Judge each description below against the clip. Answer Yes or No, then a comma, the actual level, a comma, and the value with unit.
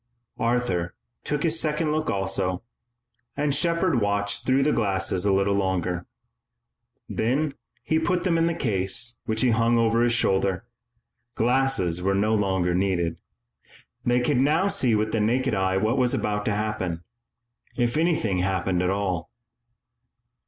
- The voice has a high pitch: No, low, 110 Hz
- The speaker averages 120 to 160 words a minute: Yes, average, 150 wpm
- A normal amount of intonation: No, wide, 5.7 semitones